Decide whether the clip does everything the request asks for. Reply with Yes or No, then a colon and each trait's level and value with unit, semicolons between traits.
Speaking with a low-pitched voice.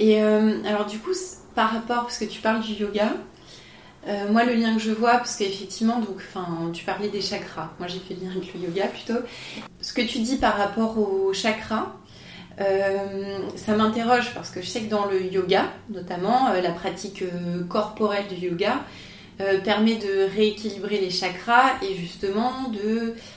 No: high, 205 Hz